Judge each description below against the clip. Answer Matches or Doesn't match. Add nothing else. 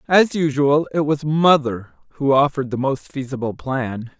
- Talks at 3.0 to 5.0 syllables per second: Matches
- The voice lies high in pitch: Doesn't match